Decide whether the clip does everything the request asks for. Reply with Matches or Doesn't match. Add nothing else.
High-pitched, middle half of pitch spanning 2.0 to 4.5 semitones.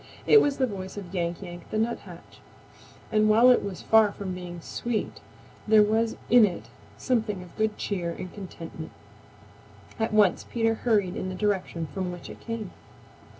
Matches